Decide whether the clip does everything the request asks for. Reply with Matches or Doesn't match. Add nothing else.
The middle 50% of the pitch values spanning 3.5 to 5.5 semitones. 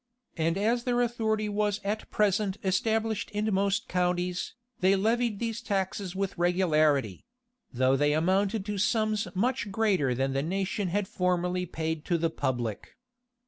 Matches